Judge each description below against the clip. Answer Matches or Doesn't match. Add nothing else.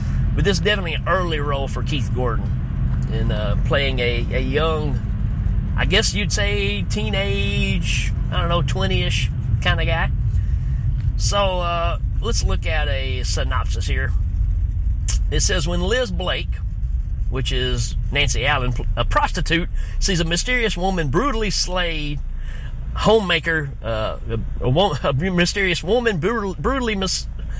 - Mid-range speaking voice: Doesn't match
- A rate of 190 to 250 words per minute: Doesn't match